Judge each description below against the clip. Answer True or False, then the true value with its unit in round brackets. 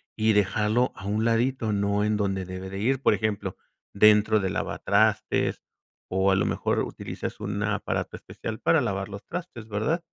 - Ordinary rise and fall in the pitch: False (2.1 semitones)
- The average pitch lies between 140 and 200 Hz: False (105 Hz)